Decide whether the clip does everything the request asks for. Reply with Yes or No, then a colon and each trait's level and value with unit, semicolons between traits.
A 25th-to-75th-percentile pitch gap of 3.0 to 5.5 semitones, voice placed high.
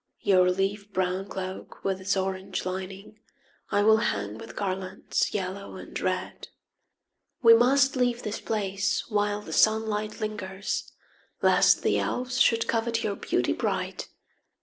No: narrow, 2.5 semitones; high, 200 Hz